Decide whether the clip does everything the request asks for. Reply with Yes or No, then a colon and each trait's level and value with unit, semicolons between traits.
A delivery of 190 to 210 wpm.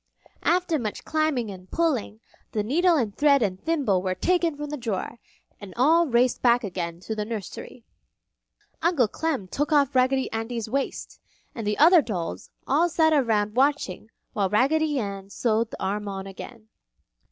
No: average, 165 wpm